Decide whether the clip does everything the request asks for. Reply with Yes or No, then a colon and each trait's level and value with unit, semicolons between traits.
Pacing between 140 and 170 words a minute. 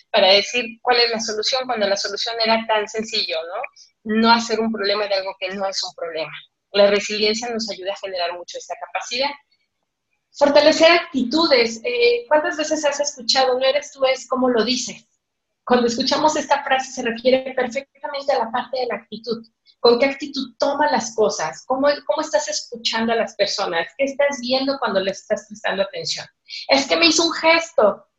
No: average, 185 wpm